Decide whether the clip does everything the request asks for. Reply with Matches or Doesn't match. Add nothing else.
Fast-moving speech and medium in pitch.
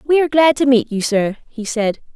Doesn't match